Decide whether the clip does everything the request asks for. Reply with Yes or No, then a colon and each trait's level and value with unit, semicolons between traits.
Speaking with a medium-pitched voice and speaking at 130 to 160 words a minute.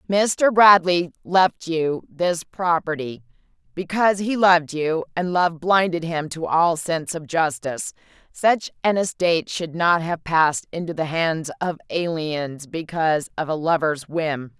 Yes: medium, 165 Hz; average, 150 wpm